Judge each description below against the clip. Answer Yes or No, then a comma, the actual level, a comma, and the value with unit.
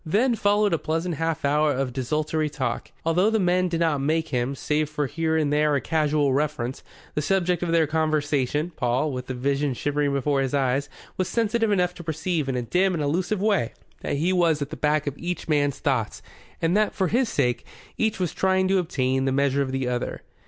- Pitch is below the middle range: No, medium, 155 Hz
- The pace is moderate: No, fast, 215 wpm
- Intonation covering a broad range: No, average, 4.2 semitones